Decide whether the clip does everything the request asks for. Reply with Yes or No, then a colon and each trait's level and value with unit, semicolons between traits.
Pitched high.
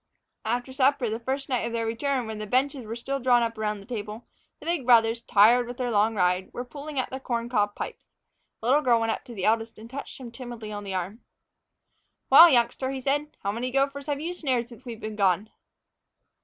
Yes: high, 235 Hz